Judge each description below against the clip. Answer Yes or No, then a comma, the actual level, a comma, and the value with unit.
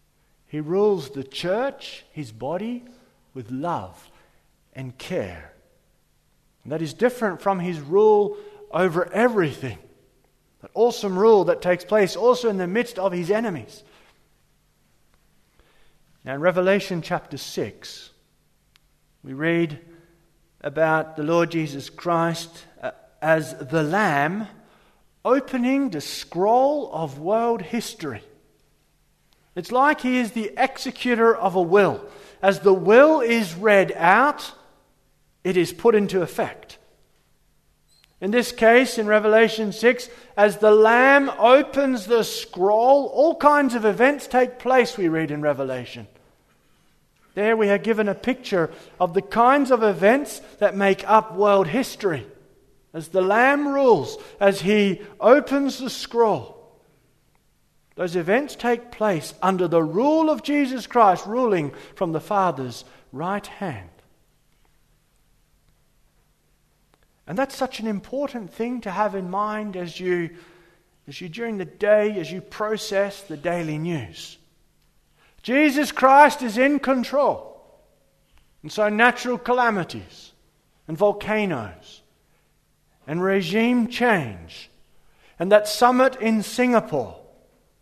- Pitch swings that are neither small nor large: No, wide, 6.1 semitones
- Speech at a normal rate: No, slow, 120 wpm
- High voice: Yes, high, 205 Hz